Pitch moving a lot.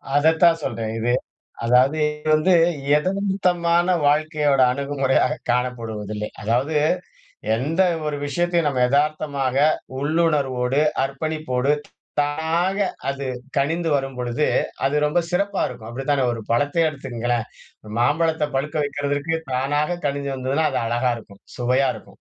No: average, 3.9 semitones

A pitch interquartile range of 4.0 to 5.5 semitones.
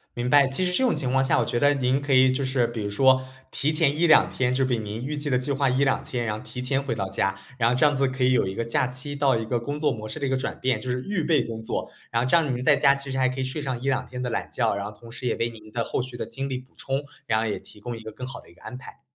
No: average, 2.8 semitones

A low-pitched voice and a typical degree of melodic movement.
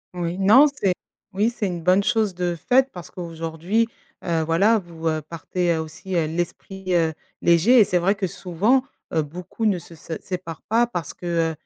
No: medium, 180 Hz; average, 3.5 semitones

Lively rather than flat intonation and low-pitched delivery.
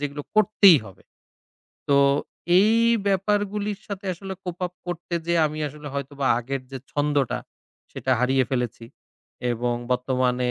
No: wide, 6.9 semitones; medium, 145 Hz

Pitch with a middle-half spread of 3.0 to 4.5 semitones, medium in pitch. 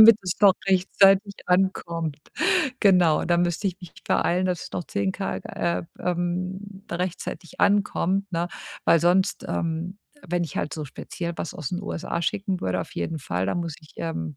No: narrow, 2.4 semitones; medium, 175 Hz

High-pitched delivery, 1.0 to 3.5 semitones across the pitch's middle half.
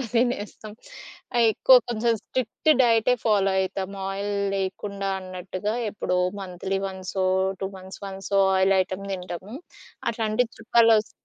Yes: high, 200 Hz; average, 2.9 semitones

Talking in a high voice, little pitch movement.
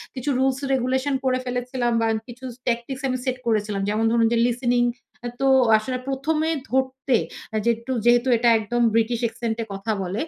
Yes: high, 240 Hz; narrow, 2.3 semitones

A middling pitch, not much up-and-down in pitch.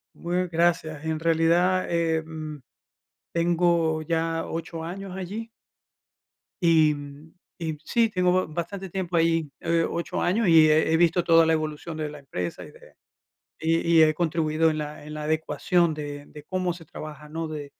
Yes: medium, 165 Hz; narrow, 2.0 semitones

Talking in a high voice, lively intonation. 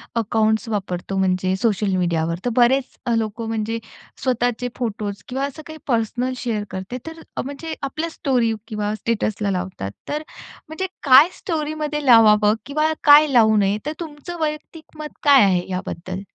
Yes: high, 230 Hz; wide, 6.0 semitones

